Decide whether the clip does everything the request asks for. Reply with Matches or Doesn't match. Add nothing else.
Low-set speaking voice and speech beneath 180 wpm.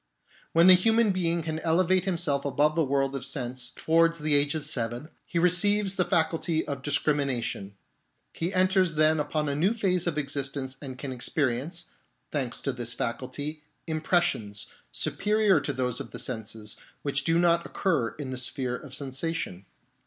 Doesn't match